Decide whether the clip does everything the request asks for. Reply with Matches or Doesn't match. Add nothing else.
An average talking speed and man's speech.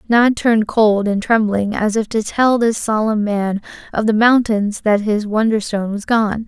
Doesn't match